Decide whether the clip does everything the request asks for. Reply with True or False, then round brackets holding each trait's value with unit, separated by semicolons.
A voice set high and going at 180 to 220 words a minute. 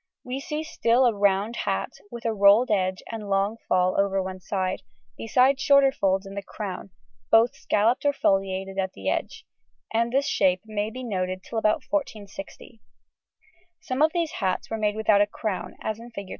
True (210 Hz; 185 wpm)